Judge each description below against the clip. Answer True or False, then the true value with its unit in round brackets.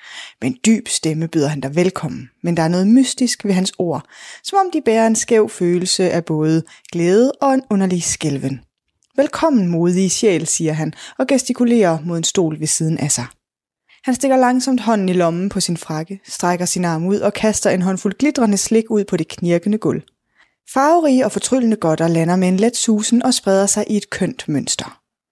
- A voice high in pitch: True (195 Hz)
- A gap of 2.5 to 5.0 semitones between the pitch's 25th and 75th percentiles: False (5.5 semitones)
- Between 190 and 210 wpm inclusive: True (195 wpm)